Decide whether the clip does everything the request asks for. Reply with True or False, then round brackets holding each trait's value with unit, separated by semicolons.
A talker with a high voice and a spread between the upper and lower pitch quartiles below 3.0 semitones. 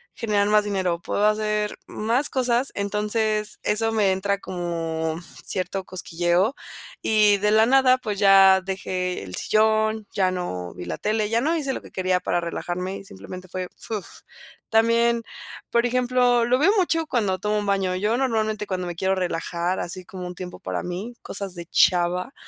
False (200 Hz; 3.6 semitones)